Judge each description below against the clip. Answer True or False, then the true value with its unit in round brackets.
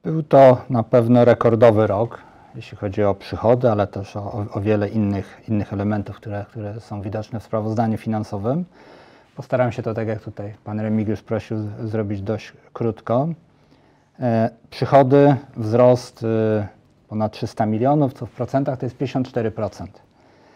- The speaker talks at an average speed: True (150 wpm)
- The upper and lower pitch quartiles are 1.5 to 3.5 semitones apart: True (2.8 semitones)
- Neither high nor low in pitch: False (115 Hz)